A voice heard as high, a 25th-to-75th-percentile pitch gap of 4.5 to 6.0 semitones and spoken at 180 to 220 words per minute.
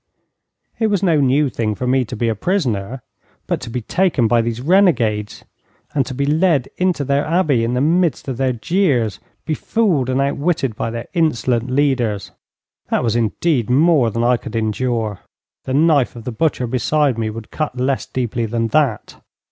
No: low, 130 Hz; average, 4.8 semitones; average, 185 wpm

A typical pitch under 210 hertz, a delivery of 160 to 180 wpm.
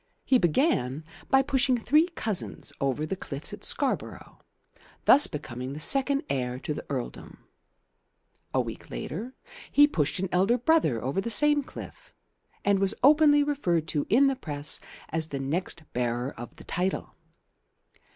No: high, 190 Hz; average, 150 wpm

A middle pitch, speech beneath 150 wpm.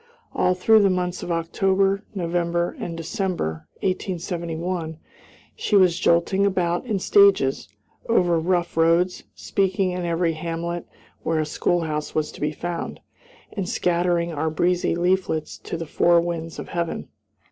Yes: medium, 175 Hz; average, 140 wpm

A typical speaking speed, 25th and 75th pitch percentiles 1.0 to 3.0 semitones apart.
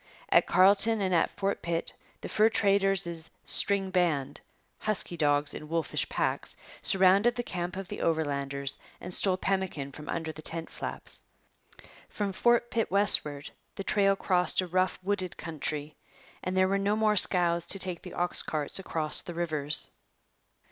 No: average, 160 wpm; average, 3.6 semitones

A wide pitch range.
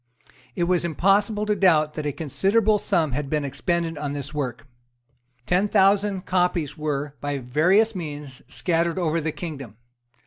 No: average, 4.5 semitones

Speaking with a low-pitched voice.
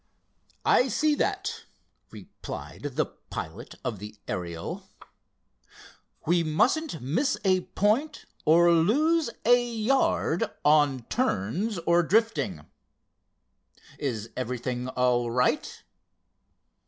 No: medium, 170 Hz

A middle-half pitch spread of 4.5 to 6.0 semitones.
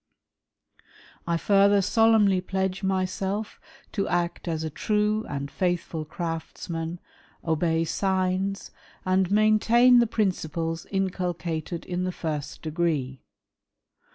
No: average, 3.2 semitones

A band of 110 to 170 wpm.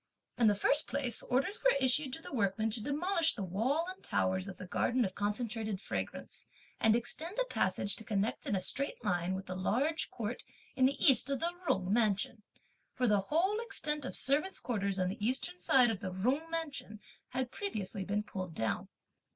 No: average, 195 wpm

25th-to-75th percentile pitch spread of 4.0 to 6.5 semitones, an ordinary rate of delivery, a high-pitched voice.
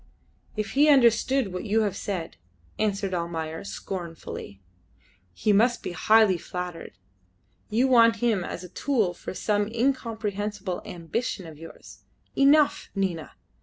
No: average, 4.5 semitones; slow, 130 wpm; high, 205 Hz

